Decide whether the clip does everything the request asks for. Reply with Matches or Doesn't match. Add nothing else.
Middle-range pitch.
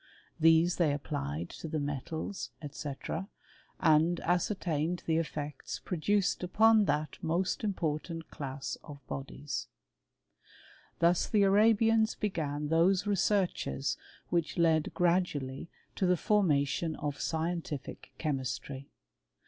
Matches